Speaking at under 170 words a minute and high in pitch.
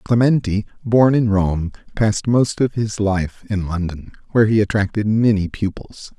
No: average, 155 wpm; low, 105 Hz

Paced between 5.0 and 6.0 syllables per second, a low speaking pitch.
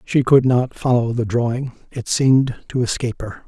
Yes: 5.1 syllables/s; low, 120 Hz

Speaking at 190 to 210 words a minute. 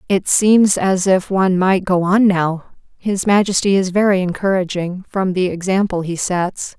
No: average, 170 wpm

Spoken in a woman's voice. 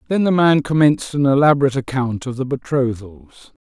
No: male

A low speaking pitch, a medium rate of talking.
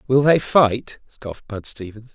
Yes: low, 120 Hz; average, 170 wpm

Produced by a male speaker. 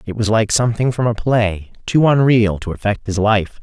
Yes: male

